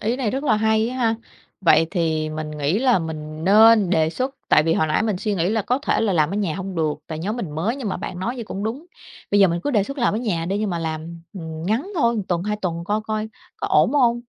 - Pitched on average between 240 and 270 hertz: No, high, 200 Hz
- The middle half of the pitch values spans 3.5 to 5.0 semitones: No, wide, 5.6 semitones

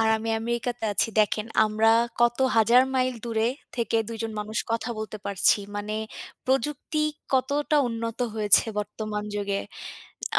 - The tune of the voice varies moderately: No, narrow, 2.1 semitones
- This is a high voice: Yes, high, 225 Hz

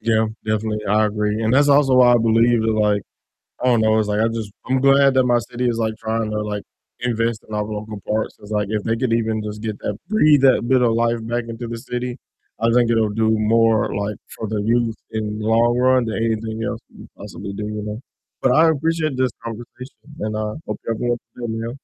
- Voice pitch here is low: Yes, low, 115 Hz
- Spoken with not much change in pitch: Yes, narrow, 2.1 semitones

